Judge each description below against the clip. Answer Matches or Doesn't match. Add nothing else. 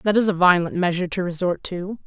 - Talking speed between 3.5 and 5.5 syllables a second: Doesn't match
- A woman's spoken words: Matches